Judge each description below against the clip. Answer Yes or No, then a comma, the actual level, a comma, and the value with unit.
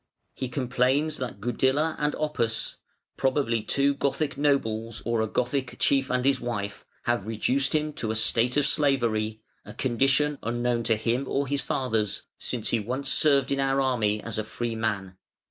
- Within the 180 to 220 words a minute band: No, average, 170 wpm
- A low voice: Yes, low, 125 Hz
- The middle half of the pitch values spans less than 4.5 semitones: Yes, average, 3.6 semitones